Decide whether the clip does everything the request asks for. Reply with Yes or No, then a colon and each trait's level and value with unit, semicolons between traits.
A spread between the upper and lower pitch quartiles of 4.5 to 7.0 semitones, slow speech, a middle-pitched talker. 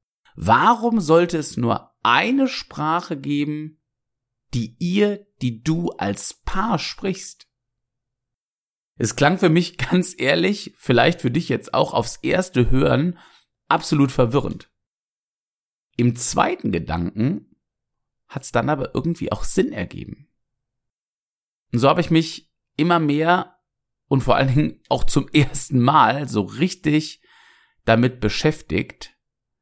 Yes: average, 5.3 semitones; slow, 120 wpm; medium, 145 Hz